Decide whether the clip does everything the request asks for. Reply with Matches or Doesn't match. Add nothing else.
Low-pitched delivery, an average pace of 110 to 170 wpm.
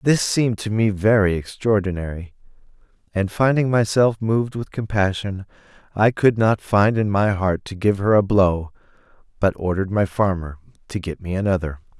Matches